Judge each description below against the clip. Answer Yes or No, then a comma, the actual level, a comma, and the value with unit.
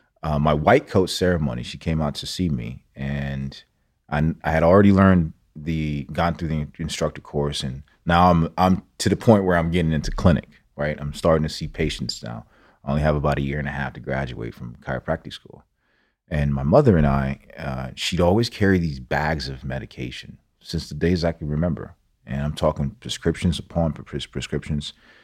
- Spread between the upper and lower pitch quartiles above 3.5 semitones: No, average, 3.0 semitones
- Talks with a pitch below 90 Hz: Yes, very low, 75 Hz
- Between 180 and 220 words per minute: Yes, average, 195 wpm